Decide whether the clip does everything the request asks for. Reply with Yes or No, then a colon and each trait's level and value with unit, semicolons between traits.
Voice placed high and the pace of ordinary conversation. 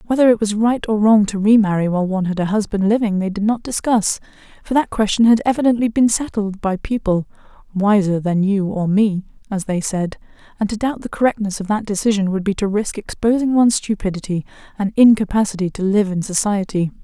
Yes: high, 205 Hz; average, 195 wpm